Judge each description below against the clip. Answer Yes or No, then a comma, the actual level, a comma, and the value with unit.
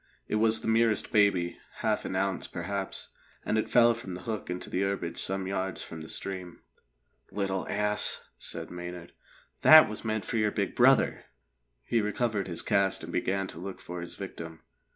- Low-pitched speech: Yes, very low, 95 Hz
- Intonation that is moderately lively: Yes, average, 3.2 semitones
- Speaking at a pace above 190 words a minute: No, average, 180 wpm